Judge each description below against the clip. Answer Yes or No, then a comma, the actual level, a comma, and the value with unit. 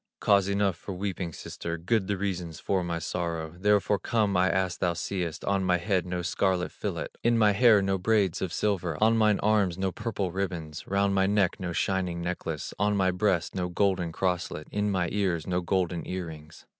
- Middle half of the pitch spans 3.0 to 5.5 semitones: No, narrow, 2.4 semitones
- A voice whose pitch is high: No, very low, 95 Hz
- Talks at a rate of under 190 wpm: No, average, 195 wpm